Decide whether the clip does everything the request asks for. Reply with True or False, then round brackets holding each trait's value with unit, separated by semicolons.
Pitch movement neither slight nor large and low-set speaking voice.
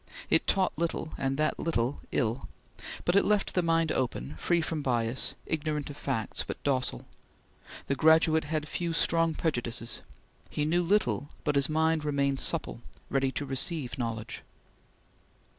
False (4.0 semitones; 150 Hz)